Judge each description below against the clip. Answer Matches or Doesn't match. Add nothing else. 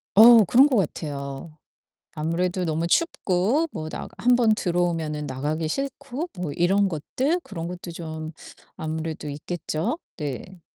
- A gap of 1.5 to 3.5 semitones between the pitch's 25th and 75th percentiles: Doesn't match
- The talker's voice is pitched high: Doesn't match